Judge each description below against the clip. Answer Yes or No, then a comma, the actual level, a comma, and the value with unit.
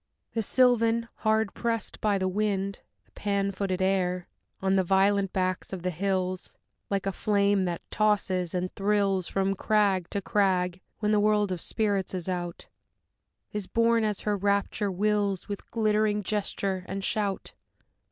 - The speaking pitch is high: Yes, high, 200 Hz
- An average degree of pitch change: No, narrow, 2.0 semitones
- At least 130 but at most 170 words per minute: Yes, average, 155 wpm